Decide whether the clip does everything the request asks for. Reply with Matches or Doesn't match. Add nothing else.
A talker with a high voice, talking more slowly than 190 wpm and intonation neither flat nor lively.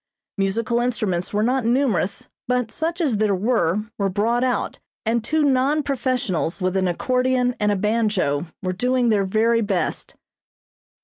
Matches